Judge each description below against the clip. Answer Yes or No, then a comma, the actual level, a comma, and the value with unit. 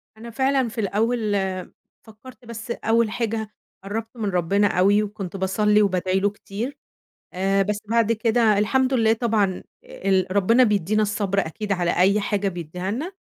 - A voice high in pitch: Yes, high, 210 Hz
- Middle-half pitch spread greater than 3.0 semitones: No, average, 2.7 semitones